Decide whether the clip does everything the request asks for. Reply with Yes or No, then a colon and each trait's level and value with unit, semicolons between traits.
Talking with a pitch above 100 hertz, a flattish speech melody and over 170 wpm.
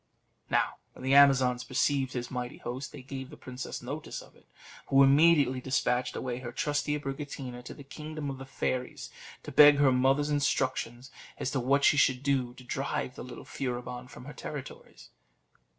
Yes: low, 135 Hz; narrow, 2.0 semitones; average, 180 wpm